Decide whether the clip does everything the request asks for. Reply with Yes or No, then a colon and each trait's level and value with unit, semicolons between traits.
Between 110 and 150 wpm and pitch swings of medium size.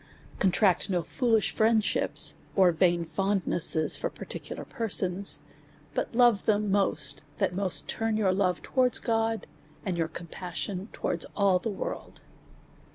Yes: average, 140 wpm; average, 3.5 semitones